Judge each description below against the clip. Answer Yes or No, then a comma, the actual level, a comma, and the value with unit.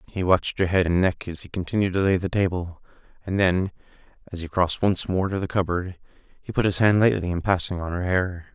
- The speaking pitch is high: No, very low, 90 Hz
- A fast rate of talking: Yes, fast, 230 wpm